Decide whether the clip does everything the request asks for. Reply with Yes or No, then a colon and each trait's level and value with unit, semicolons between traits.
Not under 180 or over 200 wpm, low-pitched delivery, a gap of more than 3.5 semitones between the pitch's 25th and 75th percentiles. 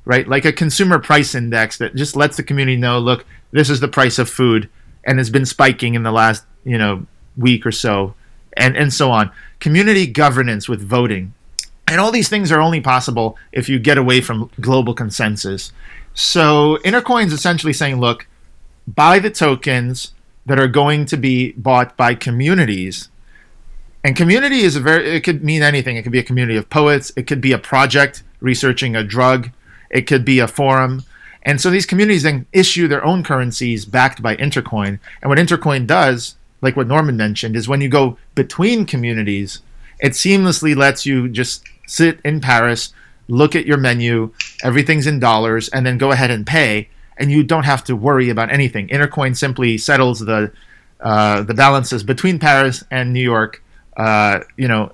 Yes: average, 185 wpm; low, 130 Hz; average, 3.9 semitones